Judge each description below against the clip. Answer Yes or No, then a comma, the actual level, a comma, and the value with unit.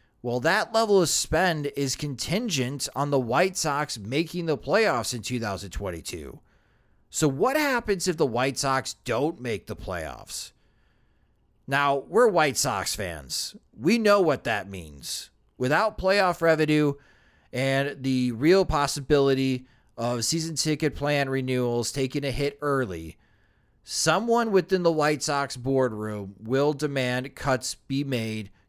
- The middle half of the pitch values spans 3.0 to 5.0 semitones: Yes, average, 4.1 semitones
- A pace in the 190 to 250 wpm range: No, slow, 135 wpm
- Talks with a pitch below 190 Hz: Yes, medium, 140 Hz